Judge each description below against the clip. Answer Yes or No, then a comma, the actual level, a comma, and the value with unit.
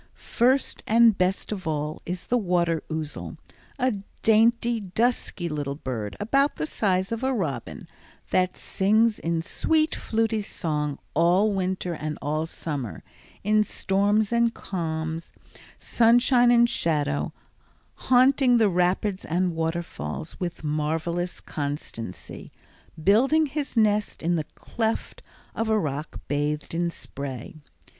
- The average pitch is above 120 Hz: Yes, medium, 185 Hz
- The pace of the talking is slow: Yes, slow, 125 wpm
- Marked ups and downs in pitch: Yes, wide, 6.2 semitones